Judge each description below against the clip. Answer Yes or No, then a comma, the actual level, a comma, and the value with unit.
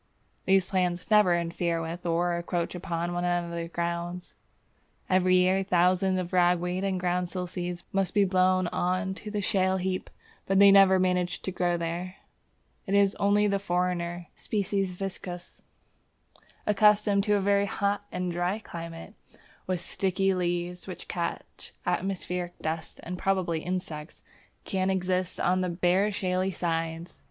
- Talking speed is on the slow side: No, average, 150 wpm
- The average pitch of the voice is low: No, medium, 180 Hz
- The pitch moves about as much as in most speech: No, narrow, 1.7 semitones